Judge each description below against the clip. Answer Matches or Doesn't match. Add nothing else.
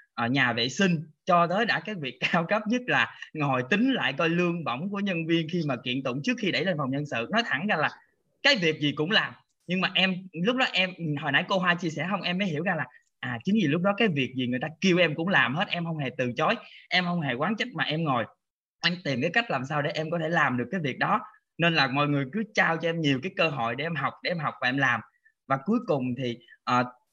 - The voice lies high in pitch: Doesn't match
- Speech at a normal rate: Doesn't match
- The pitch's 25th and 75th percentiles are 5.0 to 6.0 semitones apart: Matches